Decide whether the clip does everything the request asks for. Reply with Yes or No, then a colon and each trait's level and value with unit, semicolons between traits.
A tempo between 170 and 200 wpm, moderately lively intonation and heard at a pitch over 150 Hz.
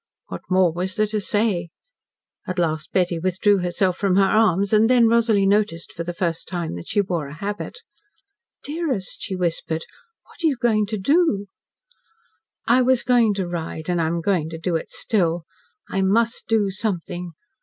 Yes: average, 180 wpm; average, 4.0 semitones; high, 190 Hz